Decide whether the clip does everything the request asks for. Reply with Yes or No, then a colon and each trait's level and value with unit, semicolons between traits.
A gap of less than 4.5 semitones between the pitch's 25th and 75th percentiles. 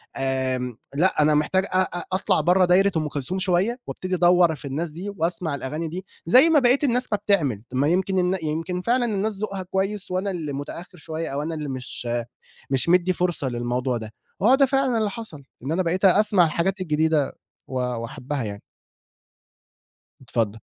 No: average, 5.2 semitones